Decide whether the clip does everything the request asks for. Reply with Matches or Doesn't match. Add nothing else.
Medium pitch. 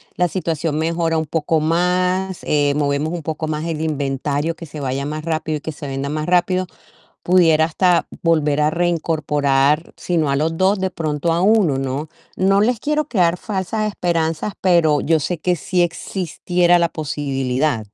Matches